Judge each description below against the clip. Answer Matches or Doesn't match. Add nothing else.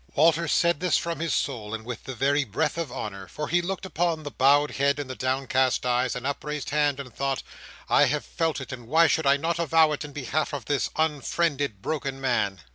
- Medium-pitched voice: Matches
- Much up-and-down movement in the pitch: Doesn't match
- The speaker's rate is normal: Doesn't match